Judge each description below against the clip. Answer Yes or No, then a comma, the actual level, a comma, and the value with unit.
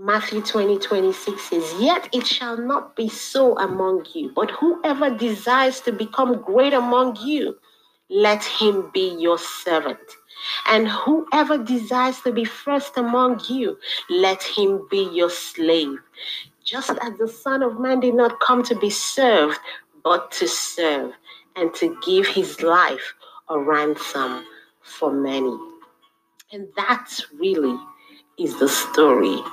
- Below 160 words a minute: Yes, average, 140 wpm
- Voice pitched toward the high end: Yes, high, 235 Hz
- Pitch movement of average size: No, wide, 6.0 semitones